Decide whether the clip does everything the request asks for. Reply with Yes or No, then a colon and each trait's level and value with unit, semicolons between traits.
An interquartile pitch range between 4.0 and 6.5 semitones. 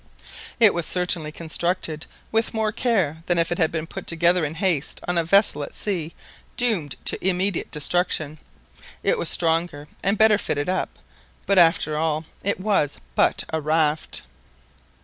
No: average, 3.5 semitones